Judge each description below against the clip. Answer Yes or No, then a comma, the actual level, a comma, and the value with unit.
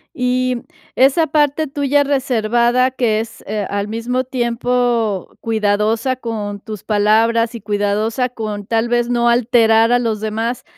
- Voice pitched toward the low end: No, high, 230 Hz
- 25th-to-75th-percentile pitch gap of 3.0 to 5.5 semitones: No, narrow, 2.6 semitones